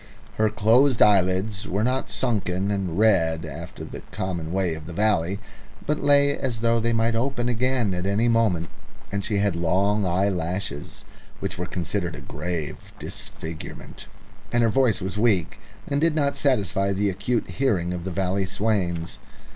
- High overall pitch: No, low, 100 Hz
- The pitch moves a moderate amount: Yes, average, 4.3 semitones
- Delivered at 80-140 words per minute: No, average, 165 wpm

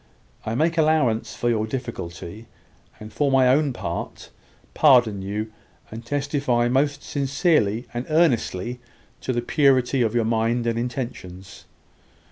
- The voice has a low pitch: Yes, low, 120 Hz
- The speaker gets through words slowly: Yes, slow, 130 wpm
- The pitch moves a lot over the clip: No, average, 3.9 semitones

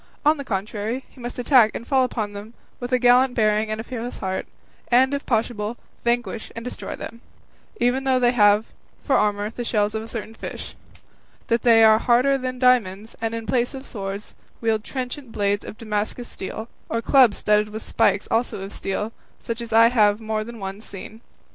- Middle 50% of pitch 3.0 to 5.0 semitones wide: No, narrow, 2.6 semitones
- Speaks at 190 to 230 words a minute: Yes, average, 200 wpm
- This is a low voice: No, high, 225 Hz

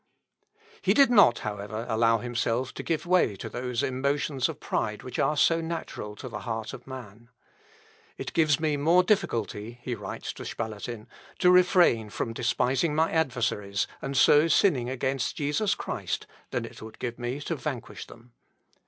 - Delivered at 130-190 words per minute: Yes, average, 165 wpm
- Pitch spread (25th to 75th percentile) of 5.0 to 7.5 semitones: Yes, wide, 5.5 semitones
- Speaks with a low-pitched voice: Yes, low, 125 Hz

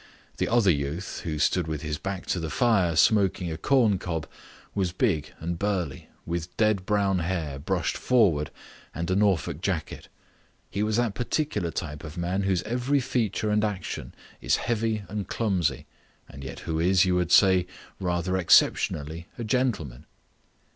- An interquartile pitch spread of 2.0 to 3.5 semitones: No, average, 4.2 semitones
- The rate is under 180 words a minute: Yes, average, 160 wpm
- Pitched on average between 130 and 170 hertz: No, very low, 95 Hz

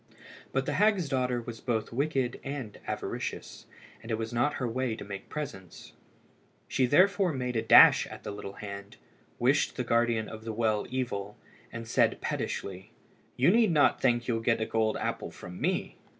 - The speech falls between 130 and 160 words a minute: No, average, 180 wpm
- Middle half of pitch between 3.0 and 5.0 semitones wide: Yes, average, 3.4 semitones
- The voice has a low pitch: Yes, low, 120 Hz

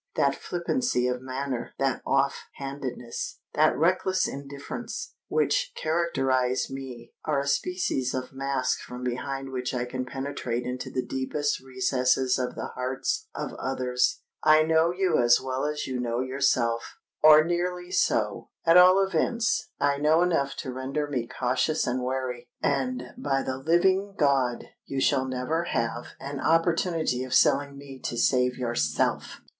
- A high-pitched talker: No, low, 135 Hz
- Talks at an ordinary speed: Yes, average, 145 wpm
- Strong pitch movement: No, average, 3.7 semitones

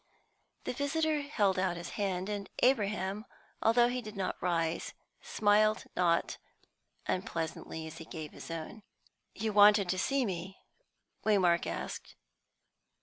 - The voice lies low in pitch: No, high, 200 Hz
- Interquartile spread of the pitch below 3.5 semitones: No, average, 3.9 semitones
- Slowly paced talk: Yes, slow, 130 wpm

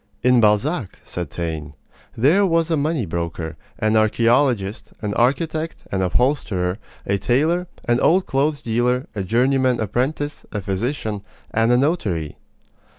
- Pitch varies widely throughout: Yes, wide, 6.3 semitones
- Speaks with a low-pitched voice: Yes, low, 120 Hz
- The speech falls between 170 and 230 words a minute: No, slow, 135 wpm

